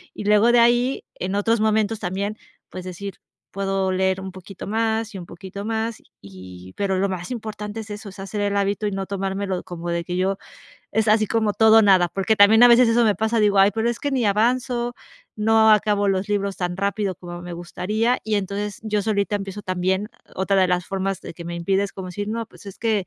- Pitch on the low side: No, high, 200 Hz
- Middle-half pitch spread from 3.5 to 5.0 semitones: No, narrow, 2.5 semitones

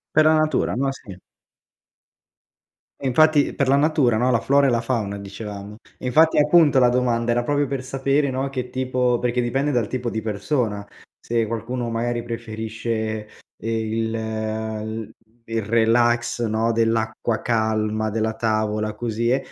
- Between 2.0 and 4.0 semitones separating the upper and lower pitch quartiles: Yes, average, 2.7 semitones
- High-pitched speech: No, low, 115 Hz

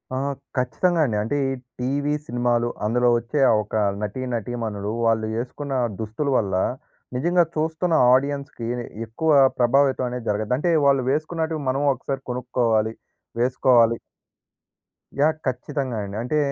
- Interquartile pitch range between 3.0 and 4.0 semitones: Yes, average, 3.6 semitones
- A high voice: No, low, 125 Hz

